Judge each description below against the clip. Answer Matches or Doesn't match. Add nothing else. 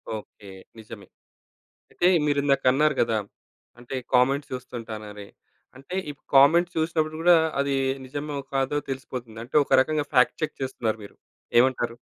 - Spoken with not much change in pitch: Doesn't match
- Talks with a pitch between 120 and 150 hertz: Matches